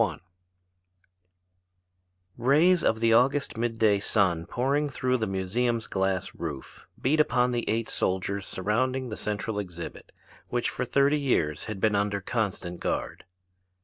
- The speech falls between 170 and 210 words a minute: No, average, 140 wpm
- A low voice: Yes, low, 110 Hz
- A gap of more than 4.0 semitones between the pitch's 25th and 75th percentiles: Yes, average, 4.8 semitones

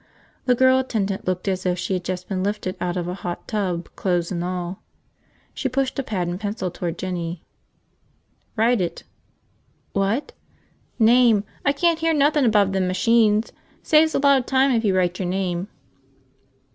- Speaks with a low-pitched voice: No, high, 195 Hz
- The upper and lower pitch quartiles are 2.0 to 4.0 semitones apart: No, wide, 5.4 semitones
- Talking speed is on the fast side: No, average, 170 wpm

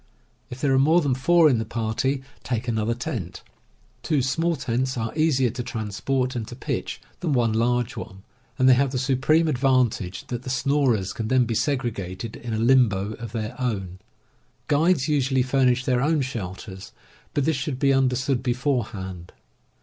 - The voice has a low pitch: Yes, low, 125 Hz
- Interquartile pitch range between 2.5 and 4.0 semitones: Yes, average, 3.3 semitones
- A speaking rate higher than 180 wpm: No, average, 170 wpm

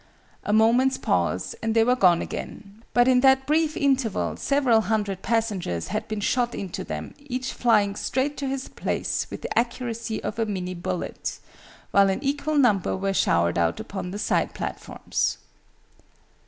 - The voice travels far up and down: No, average, 4.8 semitones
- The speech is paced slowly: No, average, 165 wpm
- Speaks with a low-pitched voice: No, high, 225 Hz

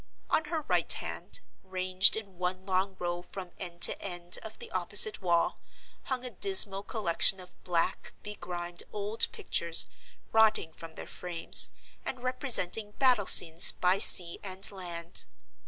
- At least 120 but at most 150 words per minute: Yes, average, 145 wpm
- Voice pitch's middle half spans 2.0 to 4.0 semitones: Yes, average, 3.3 semitones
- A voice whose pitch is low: No, medium, 185 Hz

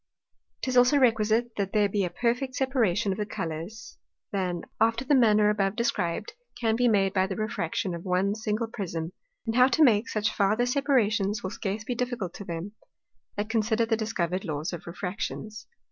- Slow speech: No, average, 180 wpm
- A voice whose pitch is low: No, high, 215 Hz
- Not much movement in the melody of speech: No, average, 3.5 semitones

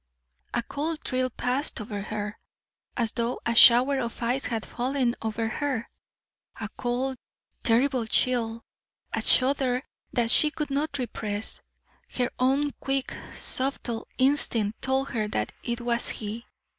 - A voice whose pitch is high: Yes, high, 245 Hz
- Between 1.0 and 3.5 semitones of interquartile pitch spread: Yes, average, 2.9 semitones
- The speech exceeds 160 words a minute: No, slow, 135 wpm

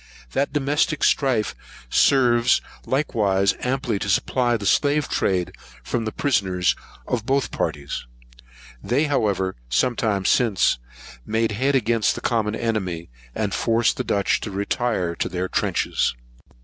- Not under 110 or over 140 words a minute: Yes, slow, 135 wpm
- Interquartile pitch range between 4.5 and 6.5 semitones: Yes, average, 4.8 semitones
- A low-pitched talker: Yes, low, 115 Hz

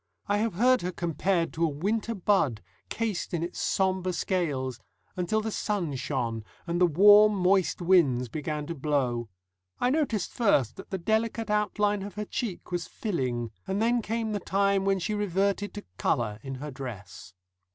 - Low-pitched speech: No, medium, 185 Hz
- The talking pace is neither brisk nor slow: Yes, average, 170 wpm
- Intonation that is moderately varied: No, wide, 6.1 semitones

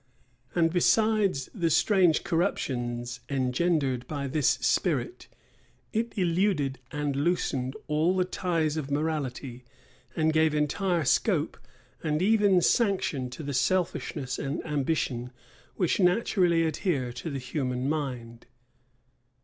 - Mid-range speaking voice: Yes, medium, 155 Hz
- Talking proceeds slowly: Yes, slow, 115 wpm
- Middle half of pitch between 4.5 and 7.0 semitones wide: Yes, average, 5.1 semitones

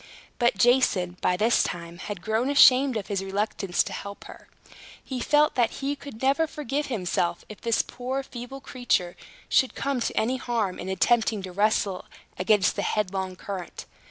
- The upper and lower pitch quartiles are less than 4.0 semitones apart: No, average, 5.3 semitones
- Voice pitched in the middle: No, high, 220 Hz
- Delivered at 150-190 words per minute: Yes, average, 170 wpm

